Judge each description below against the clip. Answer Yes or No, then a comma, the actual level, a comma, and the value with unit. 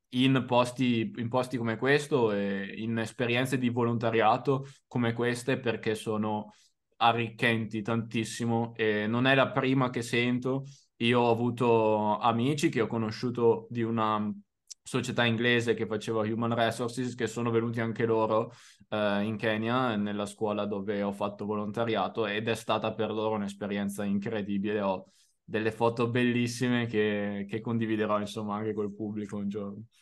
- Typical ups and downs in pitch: No, narrow, 2.2 semitones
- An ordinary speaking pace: Yes, average, 150 wpm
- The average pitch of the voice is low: Yes, low, 115 Hz